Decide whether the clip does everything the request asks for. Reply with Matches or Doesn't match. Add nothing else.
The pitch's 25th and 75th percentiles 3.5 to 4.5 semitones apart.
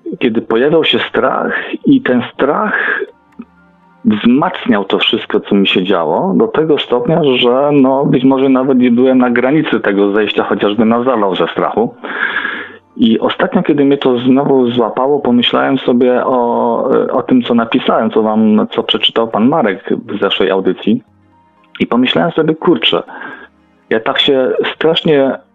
Matches